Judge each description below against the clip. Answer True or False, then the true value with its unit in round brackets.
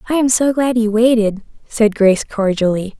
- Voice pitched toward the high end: True (220 Hz)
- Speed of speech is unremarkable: True (180 wpm)